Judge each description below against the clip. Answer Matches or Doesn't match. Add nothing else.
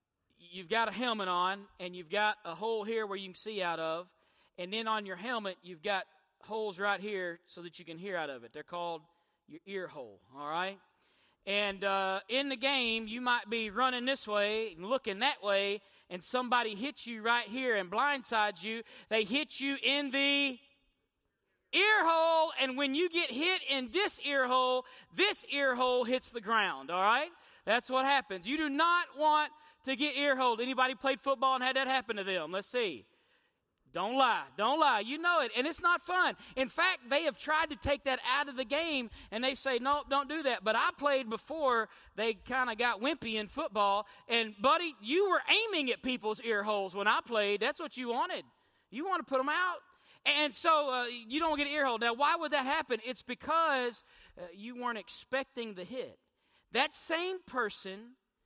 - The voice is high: Matches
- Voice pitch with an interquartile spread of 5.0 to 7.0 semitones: Matches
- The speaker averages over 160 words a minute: Matches